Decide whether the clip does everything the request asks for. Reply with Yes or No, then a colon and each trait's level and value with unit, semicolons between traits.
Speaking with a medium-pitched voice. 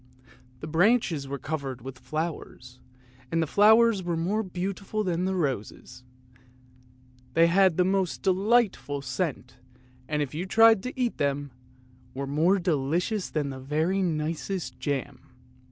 Yes: medium, 165 Hz